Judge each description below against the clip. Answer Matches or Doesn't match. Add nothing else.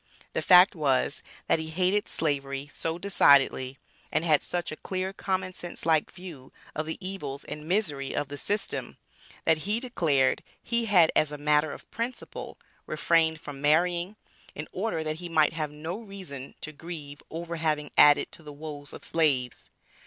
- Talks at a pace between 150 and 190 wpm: Matches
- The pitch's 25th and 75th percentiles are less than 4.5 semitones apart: Matches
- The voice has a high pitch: Doesn't match